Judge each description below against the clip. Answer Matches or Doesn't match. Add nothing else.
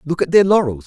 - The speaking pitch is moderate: Matches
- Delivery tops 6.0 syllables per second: Matches